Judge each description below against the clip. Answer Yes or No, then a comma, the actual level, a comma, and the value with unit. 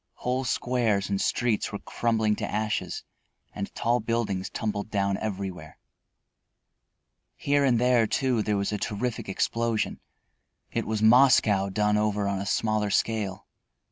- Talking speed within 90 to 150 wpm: Yes, average, 140 wpm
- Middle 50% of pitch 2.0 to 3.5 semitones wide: Yes, average, 2.7 semitones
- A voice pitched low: Yes, low, 110 Hz